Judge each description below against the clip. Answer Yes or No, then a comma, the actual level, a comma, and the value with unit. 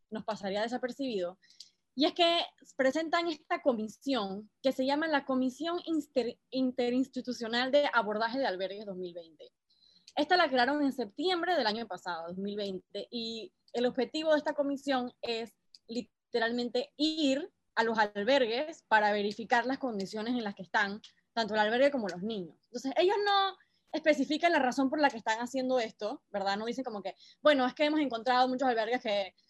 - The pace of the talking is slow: No, average, 165 wpm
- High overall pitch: Yes, very high, 250 Hz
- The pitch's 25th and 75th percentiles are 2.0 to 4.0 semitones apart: No, average, 4.8 semitones